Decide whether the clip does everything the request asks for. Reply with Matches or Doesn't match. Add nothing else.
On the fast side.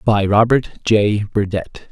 Doesn't match